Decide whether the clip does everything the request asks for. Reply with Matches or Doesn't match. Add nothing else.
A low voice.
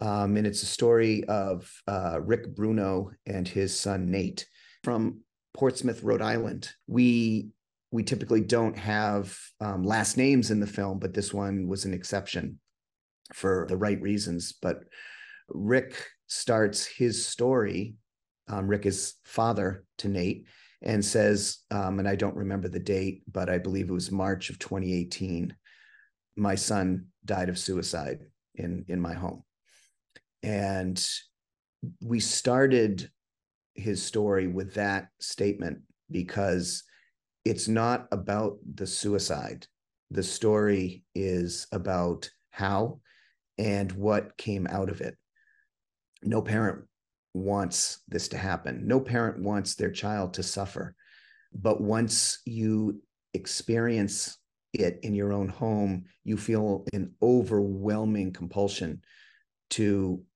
Matches